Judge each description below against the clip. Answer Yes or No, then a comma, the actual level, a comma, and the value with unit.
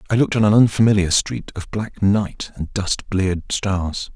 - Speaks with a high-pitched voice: No, low, 100 Hz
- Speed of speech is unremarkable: Yes, average, 190 wpm